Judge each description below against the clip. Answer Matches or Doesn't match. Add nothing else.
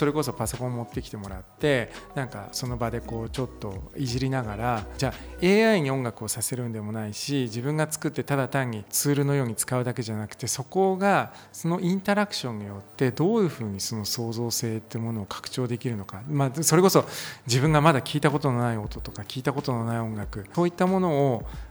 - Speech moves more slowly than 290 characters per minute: Doesn't match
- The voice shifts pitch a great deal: Doesn't match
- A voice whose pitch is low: Matches